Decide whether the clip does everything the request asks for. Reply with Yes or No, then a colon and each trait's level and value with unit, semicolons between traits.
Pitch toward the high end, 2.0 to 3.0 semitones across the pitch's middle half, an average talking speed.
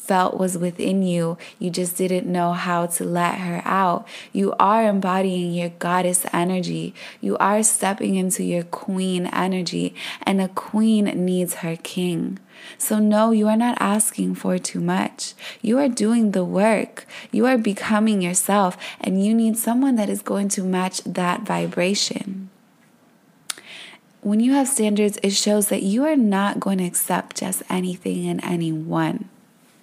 No: high, 195 Hz; average, 3.4 semitones; average, 155 wpm